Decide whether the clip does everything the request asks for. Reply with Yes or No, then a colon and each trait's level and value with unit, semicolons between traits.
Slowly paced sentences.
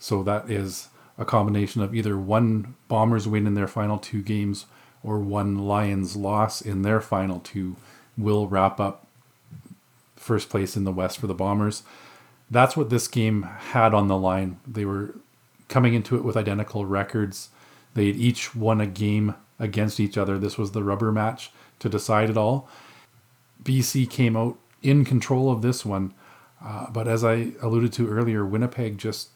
No: average, 175 wpm